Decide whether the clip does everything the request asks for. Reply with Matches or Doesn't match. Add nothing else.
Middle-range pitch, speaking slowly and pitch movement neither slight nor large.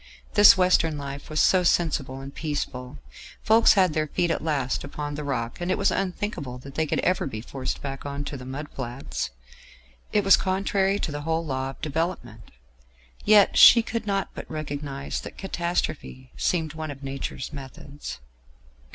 Doesn't match